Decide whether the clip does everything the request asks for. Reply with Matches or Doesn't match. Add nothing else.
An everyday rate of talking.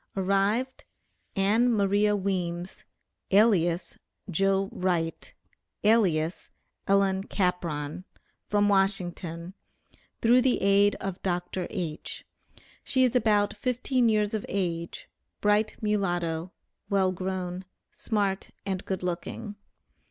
Doesn't match